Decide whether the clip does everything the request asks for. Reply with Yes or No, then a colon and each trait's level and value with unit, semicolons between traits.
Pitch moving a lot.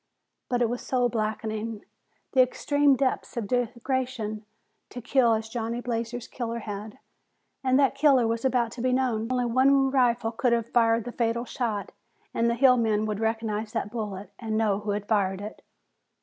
No: narrow, 2.5 semitones